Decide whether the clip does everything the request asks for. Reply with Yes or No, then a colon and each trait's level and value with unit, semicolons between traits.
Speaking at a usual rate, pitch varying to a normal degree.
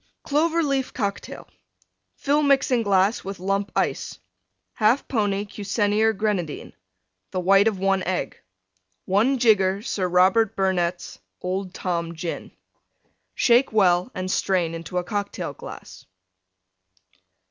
No: slow, 115 wpm; average, 3.3 semitones